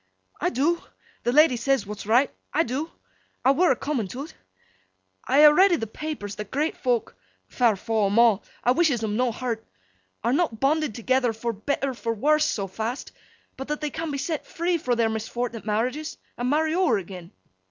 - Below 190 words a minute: No, average, 195 wpm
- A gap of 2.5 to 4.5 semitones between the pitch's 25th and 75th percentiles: No, average, 5.1 semitones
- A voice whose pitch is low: No, very high, 250 Hz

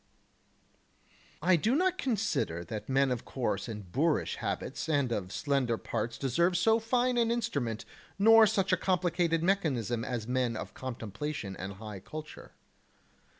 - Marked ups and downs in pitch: Yes, wide, 8.9 semitones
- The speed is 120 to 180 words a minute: Yes, average, 150 wpm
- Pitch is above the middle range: No, medium, 140 Hz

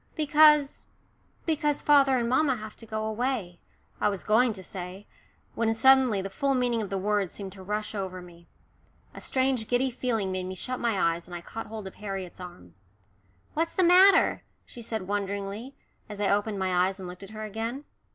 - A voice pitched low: No, high, 215 Hz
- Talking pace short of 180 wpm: No, average, 195 wpm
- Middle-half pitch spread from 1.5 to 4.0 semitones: No, average, 4.9 semitones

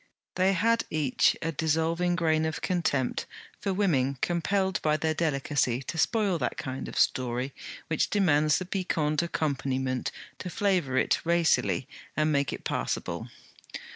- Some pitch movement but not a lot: Yes, average, 4.4 semitones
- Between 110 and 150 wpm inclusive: Yes, average, 140 wpm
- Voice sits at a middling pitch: Yes, medium, 160 Hz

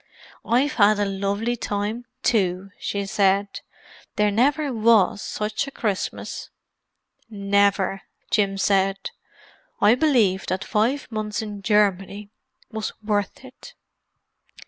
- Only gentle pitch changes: Yes, narrow, 2.3 semitones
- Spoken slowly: Yes, slow, 110 wpm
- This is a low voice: No, high, 205 Hz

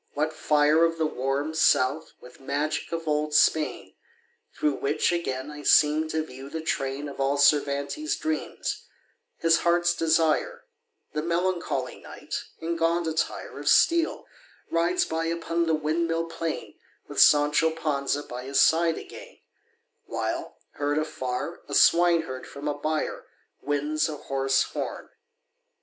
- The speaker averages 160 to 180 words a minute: No, average, 140 wpm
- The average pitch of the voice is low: No, medium, 155 Hz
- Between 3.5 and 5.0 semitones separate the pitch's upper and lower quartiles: No, narrow, 2.6 semitones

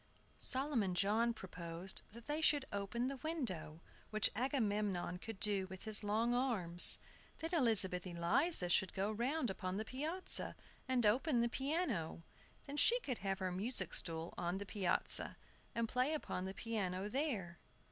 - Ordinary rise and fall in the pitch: No, wide, 5.7 semitones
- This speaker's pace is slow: No, average, 155 wpm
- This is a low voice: No, high, 215 Hz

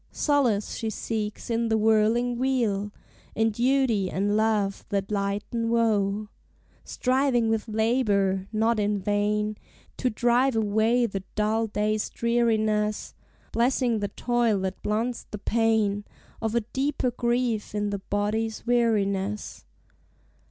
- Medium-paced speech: No, slow, 125 wpm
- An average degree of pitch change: No, narrow, 2.3 semitones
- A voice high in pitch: Yes, high, 220 Hz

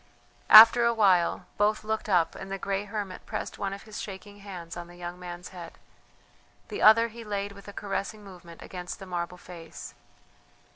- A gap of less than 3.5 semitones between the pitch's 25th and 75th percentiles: Yes, average, 2.9 semitones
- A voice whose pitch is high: Yes, high, 195 Hz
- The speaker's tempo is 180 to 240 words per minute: Yes, average, 185 wpm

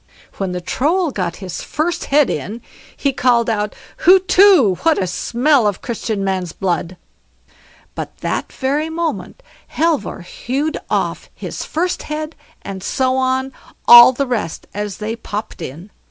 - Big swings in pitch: Yes, wide, 7.5 semitones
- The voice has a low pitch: No, high, 245 Hz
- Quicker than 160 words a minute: No, average, 145 wpm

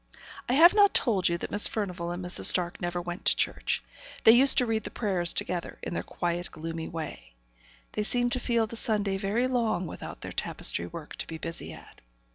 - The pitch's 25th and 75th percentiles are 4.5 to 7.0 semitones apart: Yes, average, 5.0 semitones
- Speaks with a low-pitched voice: No, high, 190 Hz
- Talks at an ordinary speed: No, fast, 210 wpm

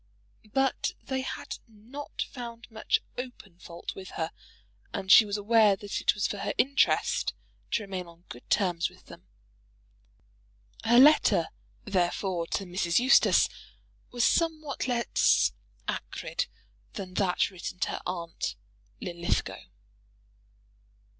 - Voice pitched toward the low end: No, high, 205 Hz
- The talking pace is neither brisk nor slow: No, slow, 125 wpm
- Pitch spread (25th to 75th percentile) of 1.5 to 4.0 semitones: No, average, 5.1 semitones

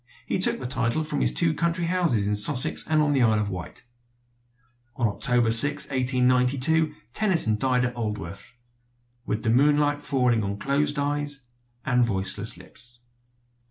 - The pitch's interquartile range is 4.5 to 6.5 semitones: Yes, average, 5.1 semitones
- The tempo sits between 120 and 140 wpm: No, average, 155 wpm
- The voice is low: Yes, low, 125 Hz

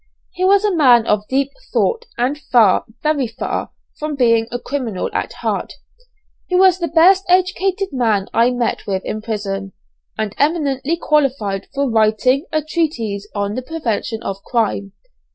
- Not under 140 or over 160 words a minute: Yes, average, 155 wpm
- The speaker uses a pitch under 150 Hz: No, very high, 255 Hz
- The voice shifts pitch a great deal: Yes, wide, 6.6 semitones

